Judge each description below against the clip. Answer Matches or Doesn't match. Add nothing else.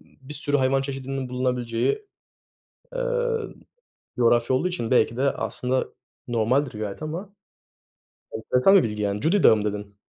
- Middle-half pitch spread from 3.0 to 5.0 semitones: Matches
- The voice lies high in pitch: Doesn't match